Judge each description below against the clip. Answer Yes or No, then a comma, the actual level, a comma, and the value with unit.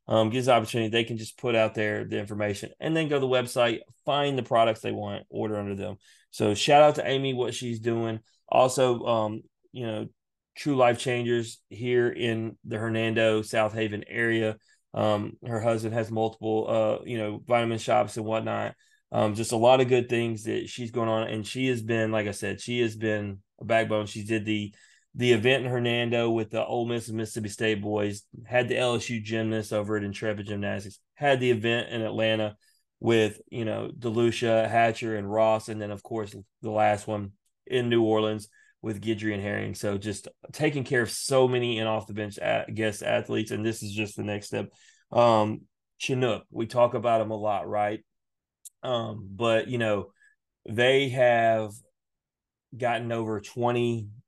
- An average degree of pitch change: No, narrow, 2.0 semitones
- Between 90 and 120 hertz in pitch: Yes, low, 110 Hz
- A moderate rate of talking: Yes, average, 185 wpm